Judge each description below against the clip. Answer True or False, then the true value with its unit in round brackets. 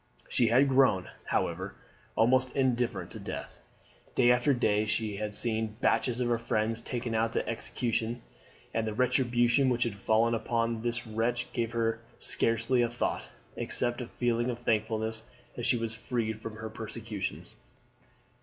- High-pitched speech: False (115 Hz)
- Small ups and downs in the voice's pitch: True (1.6 semitones)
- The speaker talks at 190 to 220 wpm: False (155 wpm)